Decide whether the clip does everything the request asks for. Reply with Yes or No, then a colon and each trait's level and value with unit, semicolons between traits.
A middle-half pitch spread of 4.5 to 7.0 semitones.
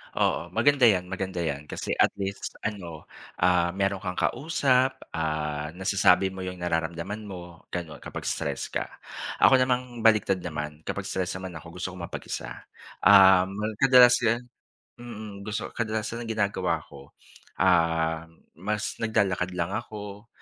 No: average, 3.9 semitones